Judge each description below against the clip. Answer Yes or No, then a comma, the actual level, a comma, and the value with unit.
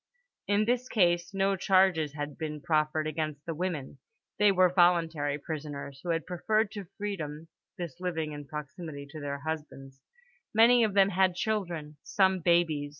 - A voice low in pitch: No, medium, 165 Hz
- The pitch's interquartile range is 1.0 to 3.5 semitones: No, average, 4.1 semitones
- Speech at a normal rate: Yes, average, 155 wpm